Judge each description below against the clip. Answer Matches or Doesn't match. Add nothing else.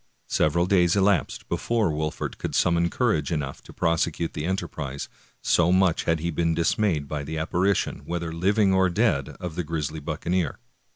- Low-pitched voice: Matches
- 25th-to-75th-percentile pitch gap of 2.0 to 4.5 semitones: Matches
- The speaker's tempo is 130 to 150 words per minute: Doesn't match